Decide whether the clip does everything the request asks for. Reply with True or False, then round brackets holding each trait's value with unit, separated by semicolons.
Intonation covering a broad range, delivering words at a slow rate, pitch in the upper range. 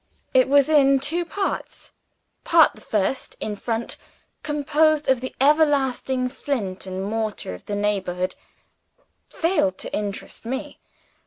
True (6.0 semitones; 130 wpm; 260 Hz)